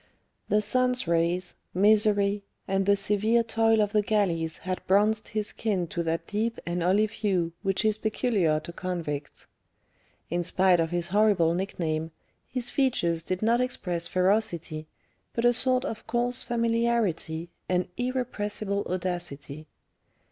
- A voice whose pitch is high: Yes, high, 200 Hz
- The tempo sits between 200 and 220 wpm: No, average, 140 wpm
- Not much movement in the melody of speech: No, average, 4.3 semitones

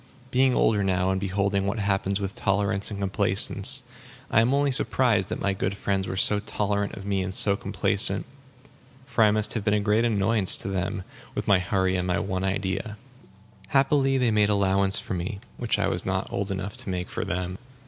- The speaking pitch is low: Yes, low, 100 Hz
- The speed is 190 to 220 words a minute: Yes, average, 200 wpm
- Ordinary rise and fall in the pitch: No, narrow, 1.8 semitones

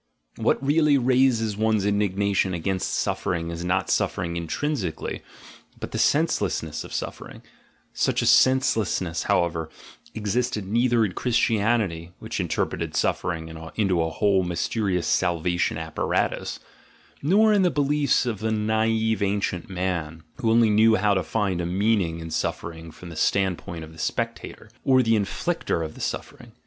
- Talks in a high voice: No, low, 100 Hz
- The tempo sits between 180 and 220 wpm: No, average, 150 wpm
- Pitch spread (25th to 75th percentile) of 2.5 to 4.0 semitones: No, average, 4.7 semitones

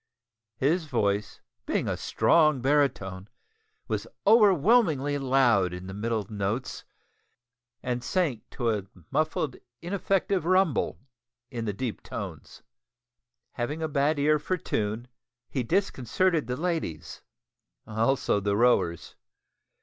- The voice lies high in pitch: No, low, 135 Hz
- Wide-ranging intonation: Yes, wide, 6.6 semitones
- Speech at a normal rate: No, slow, 110 wpm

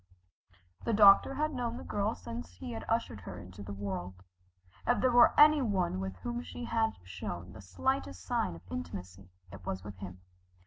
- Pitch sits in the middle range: No, low, 100 Hz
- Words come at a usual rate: Yes, average, 180 wpm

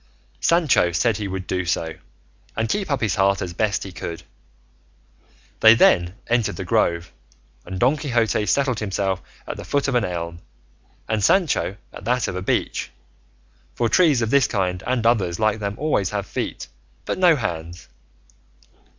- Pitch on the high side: No, low, 105 Hz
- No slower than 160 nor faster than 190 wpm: Yes, average, 170 wpm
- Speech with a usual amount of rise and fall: Yes, average, 5.0 semitones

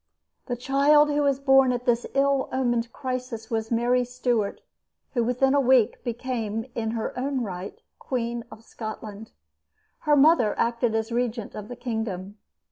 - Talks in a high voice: Yes, high, 240 Hz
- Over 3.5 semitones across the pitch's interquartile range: No, average, 2.8 semitones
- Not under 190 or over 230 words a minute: No, average, 155 wpm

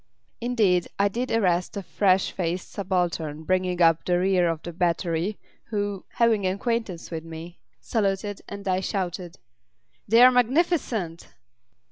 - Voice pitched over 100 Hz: Yes, medium, 185 Hz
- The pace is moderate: No, slow, 130 wpm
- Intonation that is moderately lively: Yes, average, 3.2 semitones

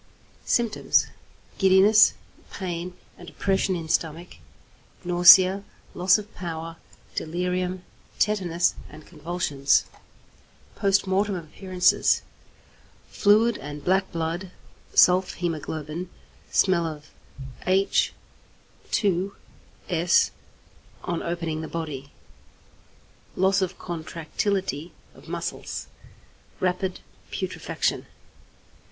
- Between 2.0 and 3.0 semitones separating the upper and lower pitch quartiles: Yes, narrow, 2.6 semitones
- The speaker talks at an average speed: No, slow, 80 wpm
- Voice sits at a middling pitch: Yes, medium, 180 Hz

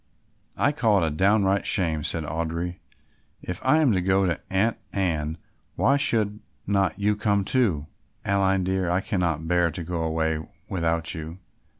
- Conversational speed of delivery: Yes, average, 165 wpm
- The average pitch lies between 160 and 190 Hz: No, very low, 90 Hz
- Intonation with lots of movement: No, average, 3.6 semitones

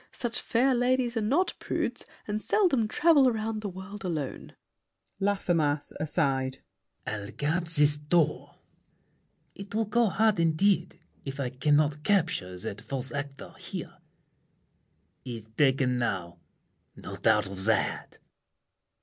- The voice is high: No, medium, 160 Hz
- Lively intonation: Yes, wide, 7.8 semitones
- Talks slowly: Yes, slow, 120 wpm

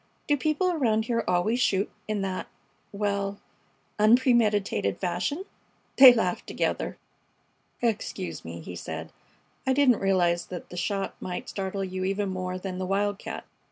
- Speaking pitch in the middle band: No, high, 200 Hz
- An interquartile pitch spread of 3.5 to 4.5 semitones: Yes, average, 3.8 semitones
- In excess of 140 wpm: No, slow, 135 wpm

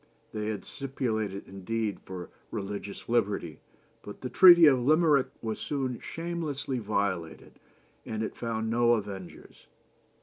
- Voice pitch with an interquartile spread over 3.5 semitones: Yes, average, 4.8 semitones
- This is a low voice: Yes, low, 115 Hz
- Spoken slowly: Yes, slow, 125 wpm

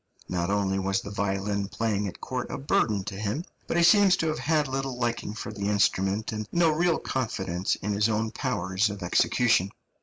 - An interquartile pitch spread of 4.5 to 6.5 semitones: Yes, average, 4.9 semitones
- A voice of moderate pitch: No, low, 105 Hz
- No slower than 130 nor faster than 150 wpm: No, average, 195 wpm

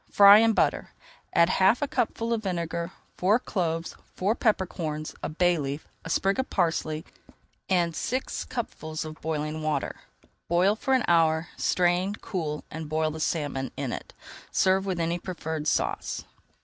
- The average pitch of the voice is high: No, medium, 170 Hz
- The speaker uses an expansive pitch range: No, average, 3.7 semitones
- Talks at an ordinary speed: Yes, average, 160 wpm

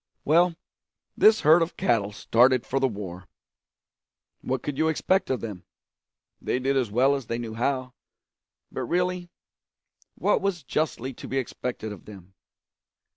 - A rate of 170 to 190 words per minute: No, average, 150 wpm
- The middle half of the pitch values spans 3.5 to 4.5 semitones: No, wide, 5.6 semitones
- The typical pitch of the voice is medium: No, low, 130 Hz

